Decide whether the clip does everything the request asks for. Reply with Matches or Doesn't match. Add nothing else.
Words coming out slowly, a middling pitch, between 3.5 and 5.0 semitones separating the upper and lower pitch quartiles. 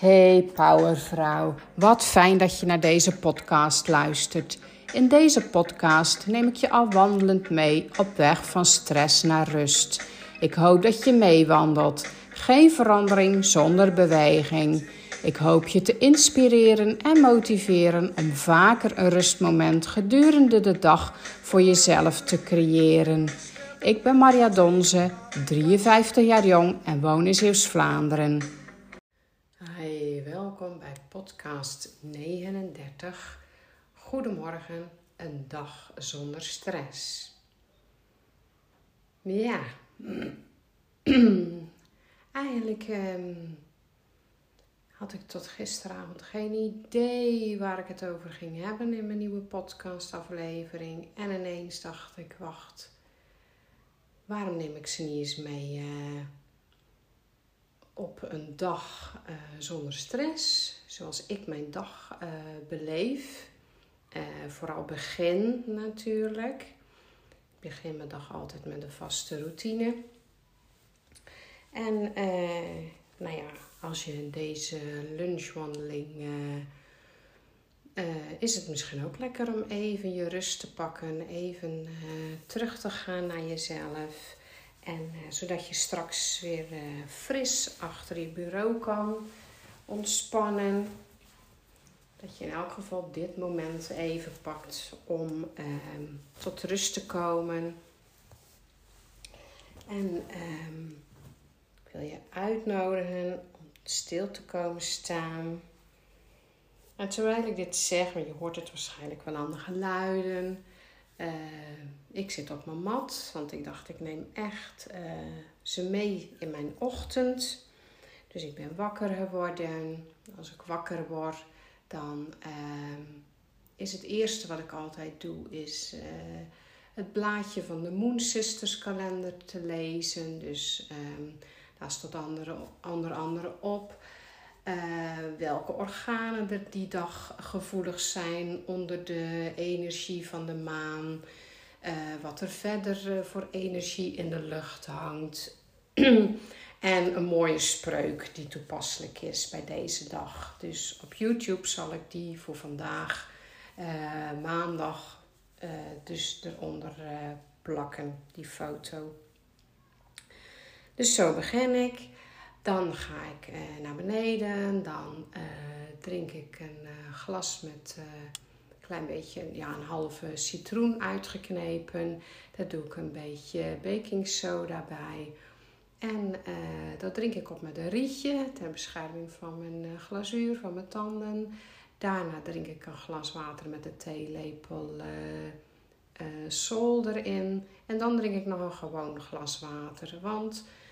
Matches